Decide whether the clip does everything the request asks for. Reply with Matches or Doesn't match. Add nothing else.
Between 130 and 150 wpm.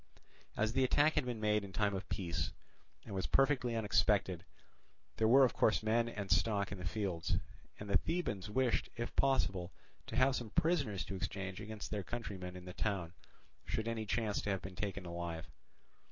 Doesn't match